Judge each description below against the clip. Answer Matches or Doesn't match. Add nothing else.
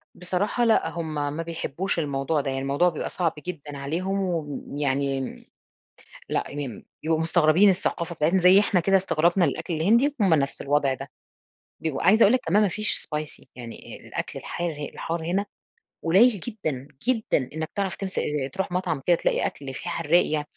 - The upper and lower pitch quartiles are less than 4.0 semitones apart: Doesn't match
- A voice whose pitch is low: Doesn't match